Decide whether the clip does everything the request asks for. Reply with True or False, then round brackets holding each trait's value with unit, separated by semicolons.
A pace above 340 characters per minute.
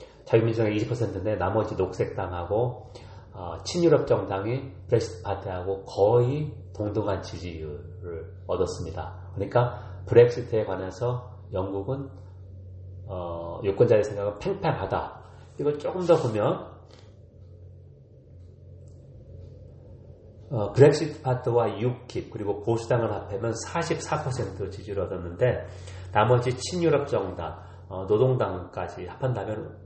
False (240 characters per minute)